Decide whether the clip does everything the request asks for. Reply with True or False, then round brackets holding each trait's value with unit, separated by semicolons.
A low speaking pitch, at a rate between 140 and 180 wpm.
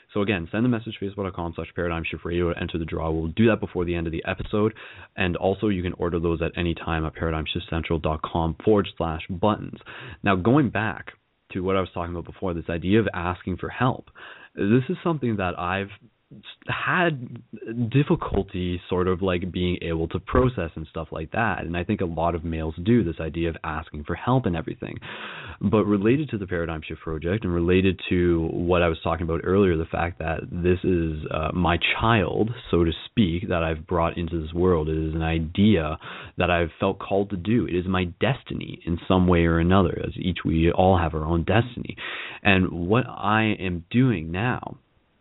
False (90 Hz; 205 wpm)